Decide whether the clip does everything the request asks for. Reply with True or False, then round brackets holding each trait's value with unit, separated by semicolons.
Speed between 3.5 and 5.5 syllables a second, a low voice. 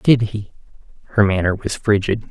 True (5.1 syllables/s; 105 Hz)